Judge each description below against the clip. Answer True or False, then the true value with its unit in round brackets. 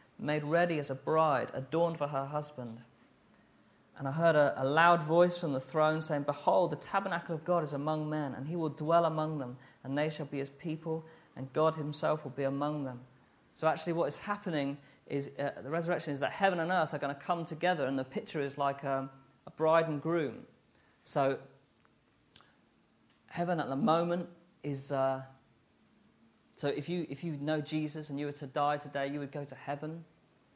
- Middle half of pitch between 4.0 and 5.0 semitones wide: False (2.8 semitones)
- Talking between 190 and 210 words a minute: True (200 wpm)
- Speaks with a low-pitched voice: False (150 Hz)